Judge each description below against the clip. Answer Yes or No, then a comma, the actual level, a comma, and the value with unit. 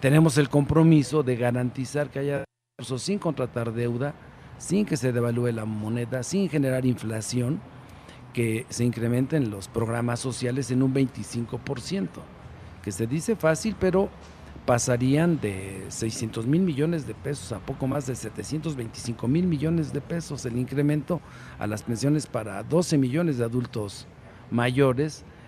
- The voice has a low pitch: Yes, low, 130 Hz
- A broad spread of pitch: No, average, 4.2 semitones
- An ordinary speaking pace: Yes, average, 145 wpm